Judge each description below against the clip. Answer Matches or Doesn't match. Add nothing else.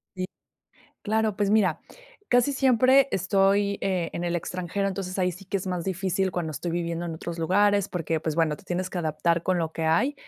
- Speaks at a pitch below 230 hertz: Matches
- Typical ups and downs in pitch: Matches